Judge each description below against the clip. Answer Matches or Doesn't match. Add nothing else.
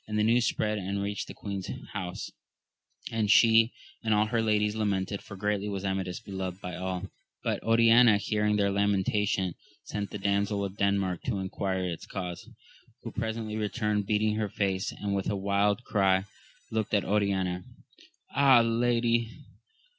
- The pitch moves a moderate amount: Doesn't match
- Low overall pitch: Matches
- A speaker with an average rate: Matches